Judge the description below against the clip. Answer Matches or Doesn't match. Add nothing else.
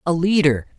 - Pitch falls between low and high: Matches